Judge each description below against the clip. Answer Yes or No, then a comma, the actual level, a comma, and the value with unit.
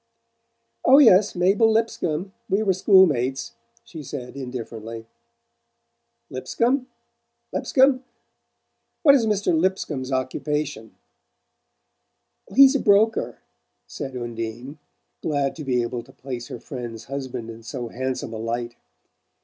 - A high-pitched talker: No, medium, 140 Hz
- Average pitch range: No, wide, 8.4 semitones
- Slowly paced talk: Yes, slow, 115 wpm